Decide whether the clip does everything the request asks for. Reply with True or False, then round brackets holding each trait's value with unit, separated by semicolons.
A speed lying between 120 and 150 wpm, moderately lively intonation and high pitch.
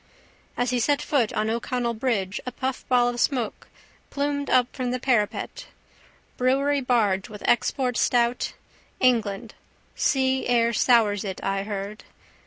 True (135 wpm; 3.2 semitones; 245 Hz)